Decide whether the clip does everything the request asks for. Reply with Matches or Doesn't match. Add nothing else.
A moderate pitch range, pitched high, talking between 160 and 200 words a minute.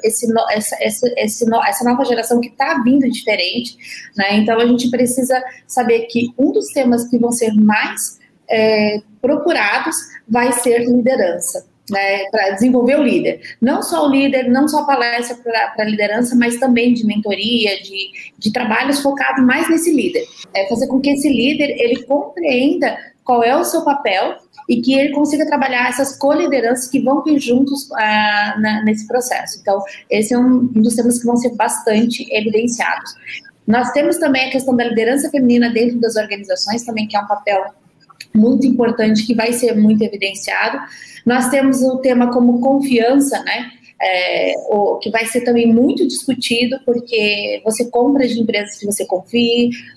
Matches